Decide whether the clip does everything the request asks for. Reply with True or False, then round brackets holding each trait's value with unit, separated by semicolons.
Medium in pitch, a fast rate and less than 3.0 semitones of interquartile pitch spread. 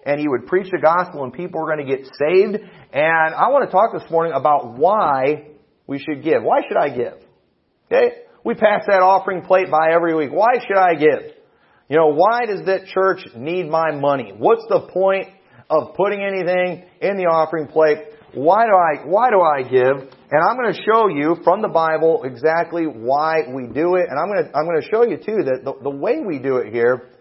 False (165 Hz; 220 wpm; 4.4 semitones)